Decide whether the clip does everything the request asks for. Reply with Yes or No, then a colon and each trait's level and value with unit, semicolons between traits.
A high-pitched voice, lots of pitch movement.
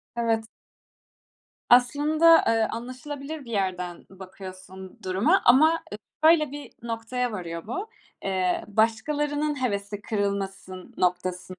Yes: high, 225 Hz; wide, 7.2 semitones